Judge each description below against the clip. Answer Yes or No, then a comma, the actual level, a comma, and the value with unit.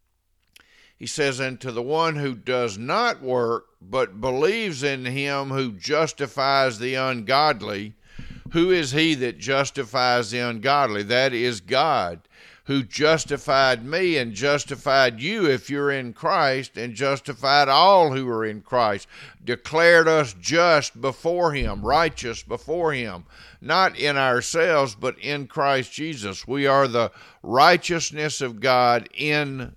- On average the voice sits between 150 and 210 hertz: No, low, 135 Hz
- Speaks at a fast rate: No, slow, 135 wpm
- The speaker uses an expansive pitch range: No, average, 3.1 semitones